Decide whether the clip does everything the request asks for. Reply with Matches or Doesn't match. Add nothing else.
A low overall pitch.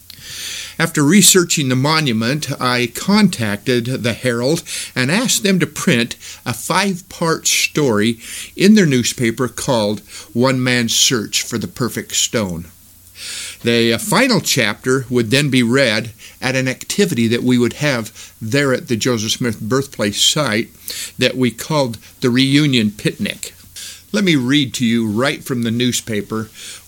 Matches